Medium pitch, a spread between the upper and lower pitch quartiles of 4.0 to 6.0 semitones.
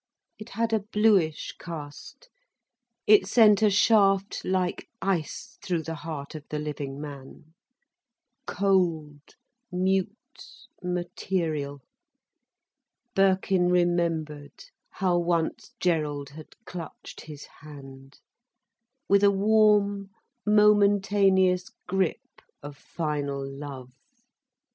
Yes: medium, 175 Hz; average, 4.8 semitones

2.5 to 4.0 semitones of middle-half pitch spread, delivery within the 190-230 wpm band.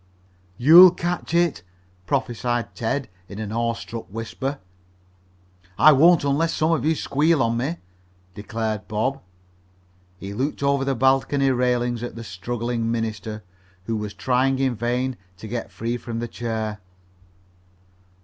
No: average, 3.4 semitones; slow, 135 wpm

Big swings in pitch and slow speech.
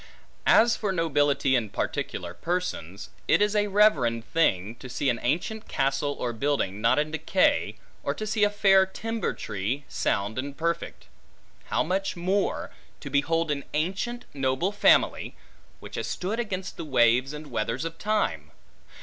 No: wide, 7.1 semitones; average, 160 wpm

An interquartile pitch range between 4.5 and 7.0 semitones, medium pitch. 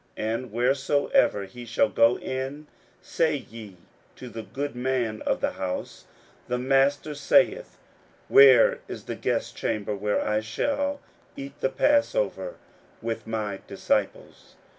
No: average, 5.0 semitones; low, 130 Hz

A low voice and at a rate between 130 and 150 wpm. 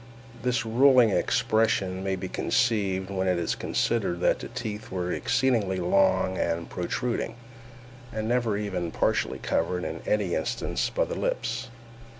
Yes: low, 105 Hz; average, 145 wpm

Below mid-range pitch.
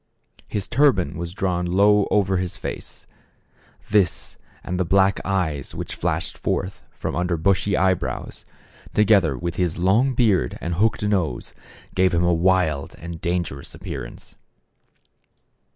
Yes: very low, 95 Hz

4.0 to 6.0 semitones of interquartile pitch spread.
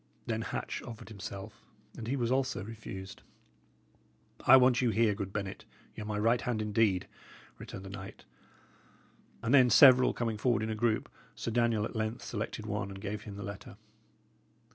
No: average, 2.7 semitones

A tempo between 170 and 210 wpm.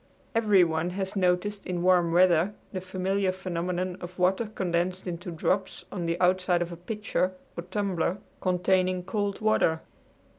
No: average, 145 wpm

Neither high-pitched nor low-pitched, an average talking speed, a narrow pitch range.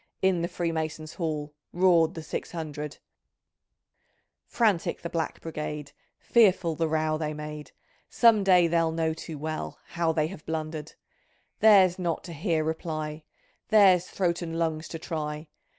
Yes: medium, 160 Hz; average, 145 wpm; narrow, 1.9 semitones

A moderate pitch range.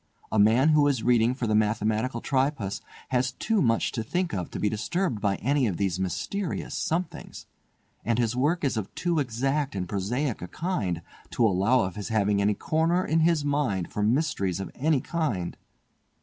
No: wide, 6.3 semitones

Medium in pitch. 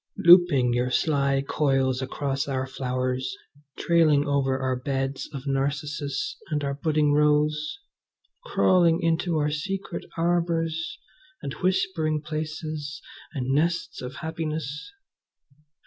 Yes: medium, 150 Hz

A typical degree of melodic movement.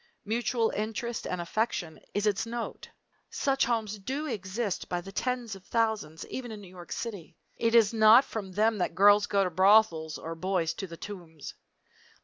Yes: average, 3.8 semitones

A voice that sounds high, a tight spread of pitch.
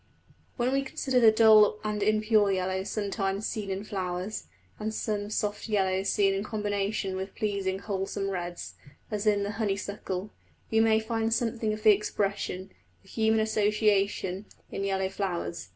Yes: high, 205 Hz; narrow, 1.9 semitones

